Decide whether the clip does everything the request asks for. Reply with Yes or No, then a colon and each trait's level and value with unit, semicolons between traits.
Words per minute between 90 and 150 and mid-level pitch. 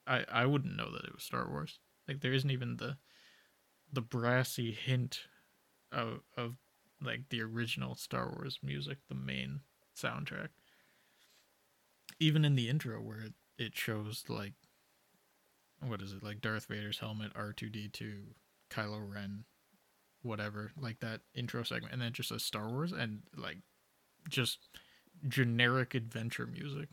No: average, 145 wpm; low, 115 Hz